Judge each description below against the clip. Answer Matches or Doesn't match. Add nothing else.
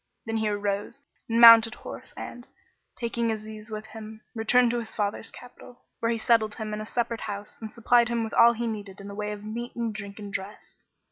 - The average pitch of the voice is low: Doesn't match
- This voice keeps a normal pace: Doesn't match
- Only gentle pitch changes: Matches